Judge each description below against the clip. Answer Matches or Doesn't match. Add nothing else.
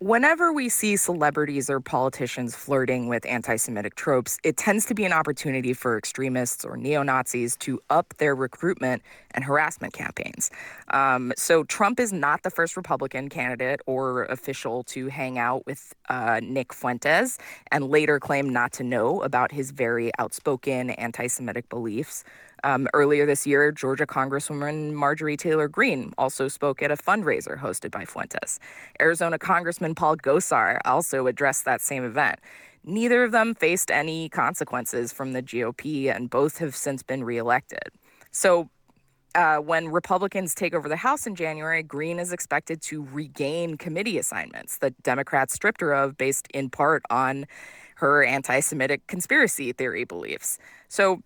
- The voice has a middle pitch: Matches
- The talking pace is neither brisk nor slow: Matches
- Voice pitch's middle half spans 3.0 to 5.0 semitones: Matches